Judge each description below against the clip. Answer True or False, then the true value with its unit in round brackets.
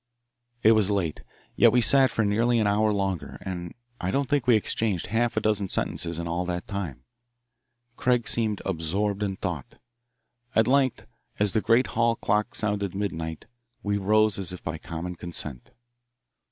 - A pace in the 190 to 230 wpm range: False (165 wpm)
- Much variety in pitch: False (3.8 semitones)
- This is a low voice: True (100 Hz)